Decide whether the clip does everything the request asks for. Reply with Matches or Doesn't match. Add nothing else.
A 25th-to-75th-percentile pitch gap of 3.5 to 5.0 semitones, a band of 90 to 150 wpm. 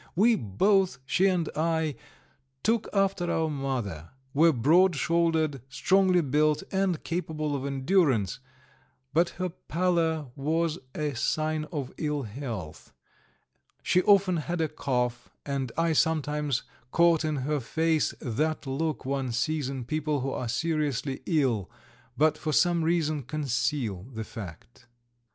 Matches